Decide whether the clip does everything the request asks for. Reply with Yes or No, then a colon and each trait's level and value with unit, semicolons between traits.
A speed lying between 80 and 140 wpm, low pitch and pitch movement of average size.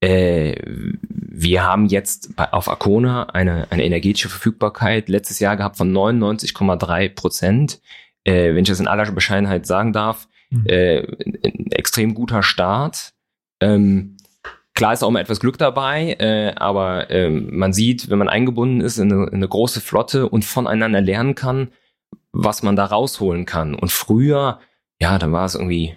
No: average, 160 wpm; low, 100 Hz; average, 3.2 semitones